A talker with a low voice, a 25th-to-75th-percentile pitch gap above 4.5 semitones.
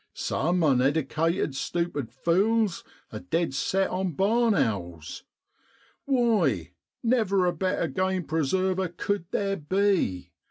No: medium, 175 Hz; wide, 5.4 semitones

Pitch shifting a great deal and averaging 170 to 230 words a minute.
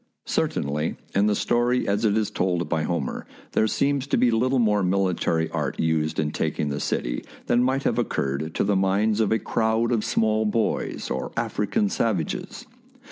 Yes: wide, 5.7 semitones; average, 180 wpm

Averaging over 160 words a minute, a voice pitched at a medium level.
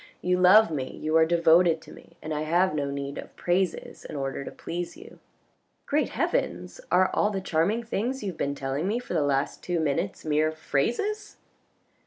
Yes: average, 200 wpm; medium, 170 Hz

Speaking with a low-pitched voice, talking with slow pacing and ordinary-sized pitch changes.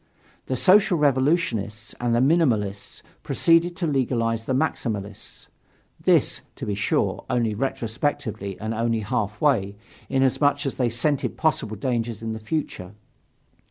Yes: low, 120 Hz; slow, 130 wpm; average, 4.7 semitones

